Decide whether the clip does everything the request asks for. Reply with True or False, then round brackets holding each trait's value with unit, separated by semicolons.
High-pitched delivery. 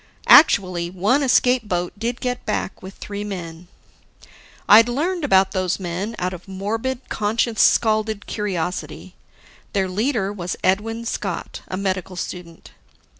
True (200 Hz)